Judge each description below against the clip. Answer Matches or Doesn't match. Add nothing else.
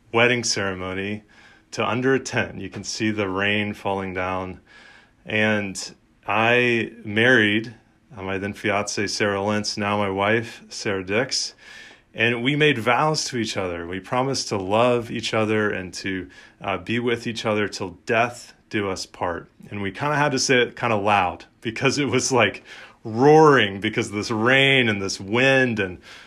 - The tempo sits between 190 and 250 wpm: Doesn't match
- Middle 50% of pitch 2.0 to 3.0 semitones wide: Doesn't match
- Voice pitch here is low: Matches